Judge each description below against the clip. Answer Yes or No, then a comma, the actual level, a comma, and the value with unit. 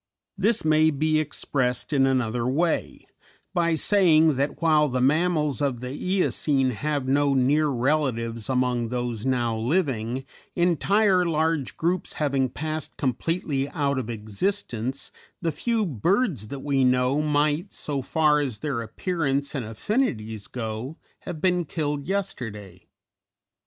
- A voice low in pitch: No, medium, 145 Hz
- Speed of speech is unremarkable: No, slow, 130 wpm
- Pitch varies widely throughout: No, average, 4.2 semitones